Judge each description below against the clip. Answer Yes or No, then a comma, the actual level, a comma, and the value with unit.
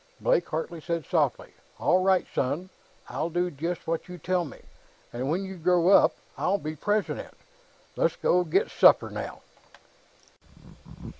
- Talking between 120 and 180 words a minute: Yes, average, 145 wpm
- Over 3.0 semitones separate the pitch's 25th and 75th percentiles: No, narrow, 2.5 semitones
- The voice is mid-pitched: Yes, medium, 175 Hz